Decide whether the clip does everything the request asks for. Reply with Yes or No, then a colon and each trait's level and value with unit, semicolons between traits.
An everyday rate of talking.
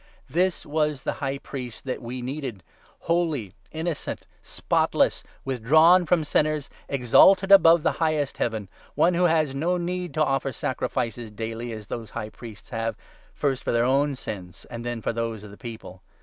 Yes: average, 180 wpm